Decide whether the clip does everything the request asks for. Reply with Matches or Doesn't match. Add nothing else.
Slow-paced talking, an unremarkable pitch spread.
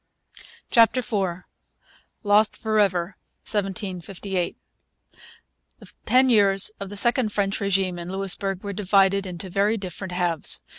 Doesn't match